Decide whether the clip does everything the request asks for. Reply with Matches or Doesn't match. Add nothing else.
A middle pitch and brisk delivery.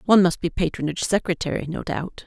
Doesn't match